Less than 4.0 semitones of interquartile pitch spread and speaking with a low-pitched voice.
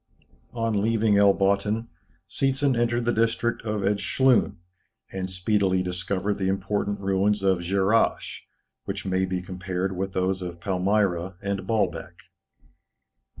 Yes: narrow, 2.5 semitones; low, 100 Hz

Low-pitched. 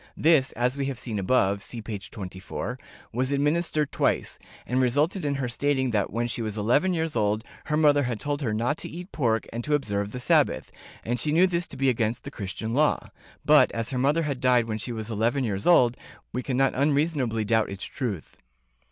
Yes: low, 125 Hz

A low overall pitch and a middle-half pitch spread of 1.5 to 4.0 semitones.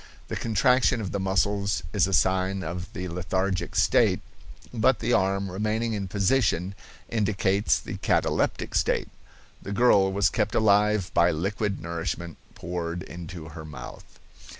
Yes: very low, 95 Hz; average, 2.9 semitones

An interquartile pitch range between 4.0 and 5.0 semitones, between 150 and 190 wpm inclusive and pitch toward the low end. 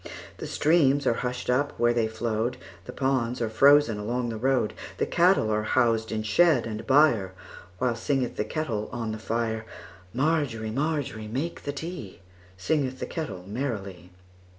No: average, 4.4 semitones; average, 140 wpm; low, 120 Hz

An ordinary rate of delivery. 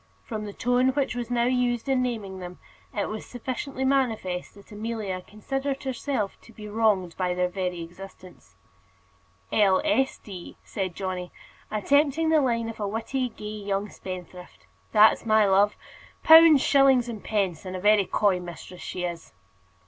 Yes: average, 160 wpm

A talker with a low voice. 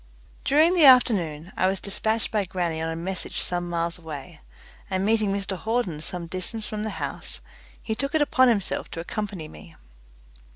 No: high, 190 Hz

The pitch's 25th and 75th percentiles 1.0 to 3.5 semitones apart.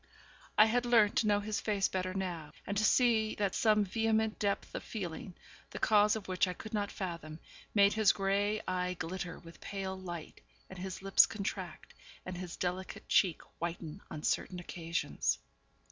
Yes: average, 2.9 semitones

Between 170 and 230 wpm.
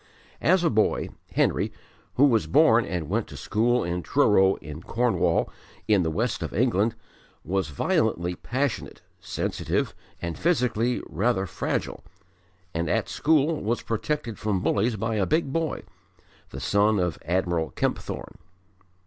No: average, 140 wpm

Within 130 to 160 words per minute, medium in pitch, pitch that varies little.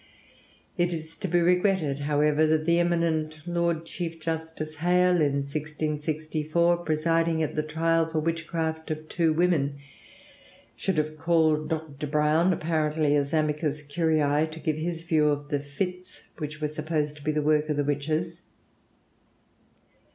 Yes: average, 150 wpm; medium, 155 Hz; narrow, 1.6 semitones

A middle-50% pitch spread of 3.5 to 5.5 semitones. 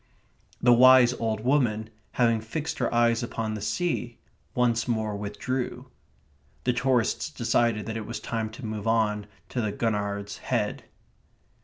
No: narrow, 2.4 semitones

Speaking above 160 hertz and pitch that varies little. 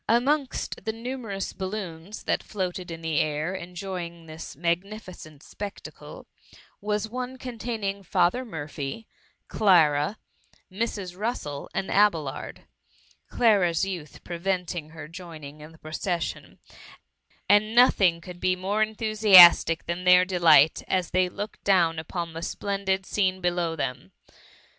No: medium, 185 Hz; average, 3.9 semitones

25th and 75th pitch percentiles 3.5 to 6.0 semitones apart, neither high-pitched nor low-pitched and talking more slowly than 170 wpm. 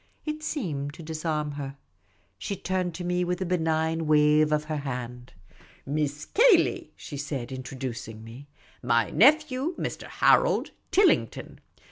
Yes: average, 4.5 semitones; medium, 155 Hz; average, 150 wpm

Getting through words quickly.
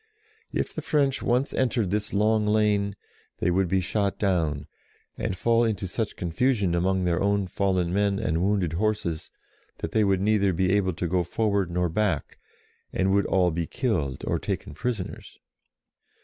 No: average, 165 wpm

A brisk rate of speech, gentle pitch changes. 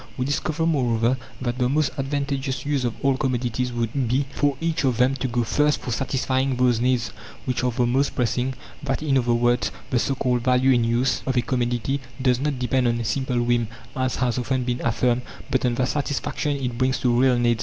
Yes: fast, 215 wpm; narrow, 1.9 semitones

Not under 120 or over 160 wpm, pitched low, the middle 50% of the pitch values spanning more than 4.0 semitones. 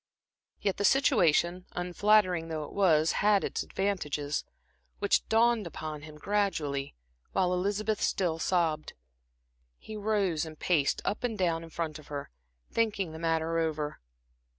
No: average, 140 wpm; medium, 175 Hz; average, 4.4 semitones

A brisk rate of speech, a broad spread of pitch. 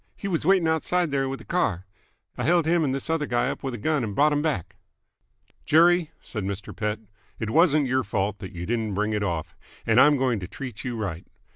Yes: fast, 230 wpm; wide, 6.9 semitones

